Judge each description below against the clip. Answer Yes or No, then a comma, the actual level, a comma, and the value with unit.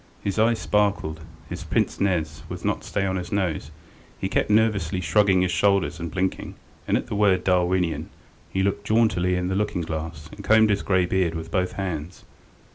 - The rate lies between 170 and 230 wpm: Yes, average, 190 wpm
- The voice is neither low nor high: No, very low, 95 Hz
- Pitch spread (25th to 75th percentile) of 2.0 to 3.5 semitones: Yes, average, 3.0 semitones